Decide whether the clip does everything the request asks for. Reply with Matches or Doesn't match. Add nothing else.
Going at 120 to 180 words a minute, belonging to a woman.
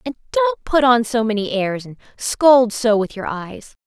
Doesn't match